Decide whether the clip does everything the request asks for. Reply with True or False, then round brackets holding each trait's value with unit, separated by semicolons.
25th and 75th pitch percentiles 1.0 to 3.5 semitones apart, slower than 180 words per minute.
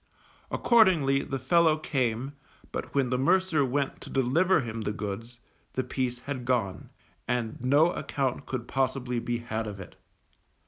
True (3.0 semitones; 150 wpm)